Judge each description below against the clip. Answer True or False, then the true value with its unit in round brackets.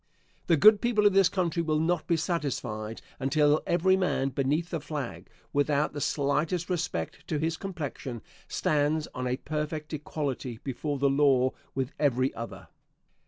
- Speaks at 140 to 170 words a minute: True (155 wpm)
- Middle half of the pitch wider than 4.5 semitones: False (3.7 semitones)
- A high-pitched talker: False (150 Hz)